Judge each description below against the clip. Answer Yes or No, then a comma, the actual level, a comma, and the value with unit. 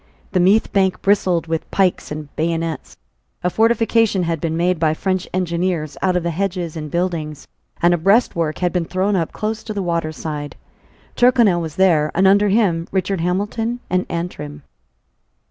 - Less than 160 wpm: No, average, 175 wpm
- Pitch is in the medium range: Yes, medium, 180 Hz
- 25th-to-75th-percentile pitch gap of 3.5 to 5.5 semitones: No, average, 3.0 semitones